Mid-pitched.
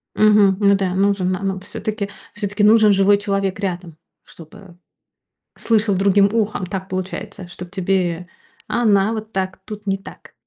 No: high, 195 Hz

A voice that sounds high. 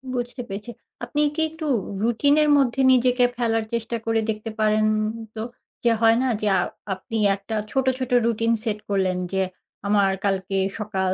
Yes: high, 225 Hz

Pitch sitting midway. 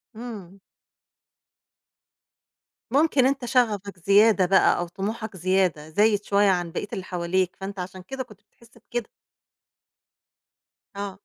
No: high, 200 Hz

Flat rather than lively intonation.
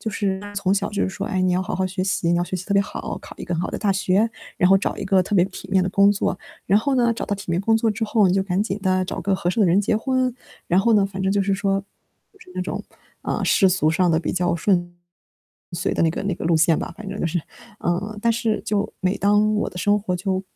Yes: narrow, 2.1 semitones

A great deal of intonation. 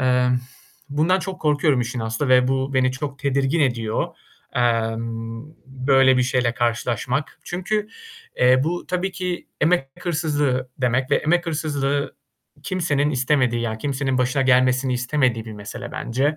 No: average, 3.2 semitones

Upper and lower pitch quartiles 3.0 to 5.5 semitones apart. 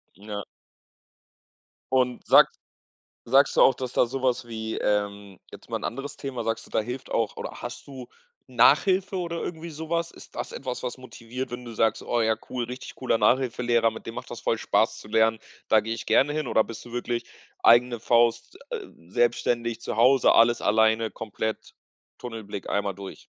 No: narrow, 2.6 semitones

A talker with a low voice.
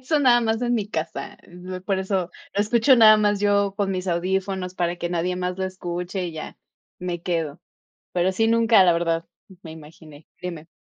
No: medium, 185 Hz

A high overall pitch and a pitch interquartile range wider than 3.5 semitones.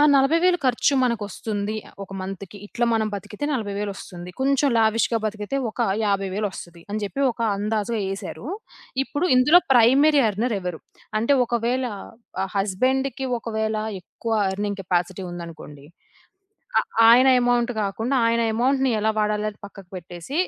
Yes: high, 220 Hz; average, 4.1 semitones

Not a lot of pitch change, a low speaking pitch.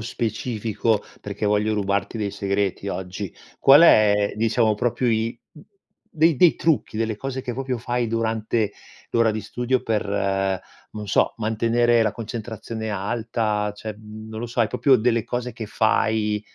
Yes: narrow, 2.1 semitones; low, 110 Hz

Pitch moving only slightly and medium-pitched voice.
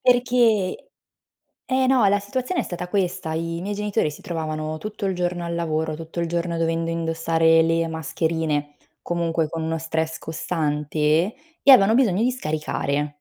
No: average, 3.6 semitones; medium, 165 Hz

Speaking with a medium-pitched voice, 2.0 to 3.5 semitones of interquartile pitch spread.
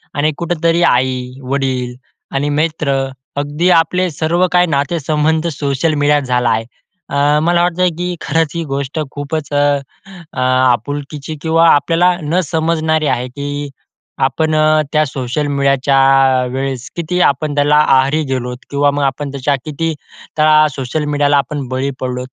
Yes: medium, 145 Hz; average, 2.8 semitones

